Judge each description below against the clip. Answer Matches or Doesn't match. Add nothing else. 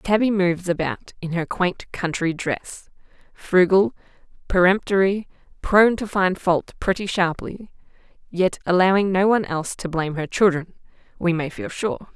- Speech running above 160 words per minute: Doesn't match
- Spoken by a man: Doesn't match